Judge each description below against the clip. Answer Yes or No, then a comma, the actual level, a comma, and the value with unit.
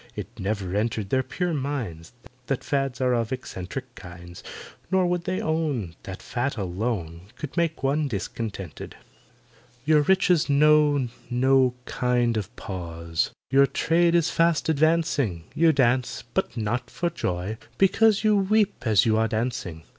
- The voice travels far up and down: Yes, wide, 7.0 semitones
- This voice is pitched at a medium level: No, low, 125 Hz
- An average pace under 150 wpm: Yes, average, 140 wpm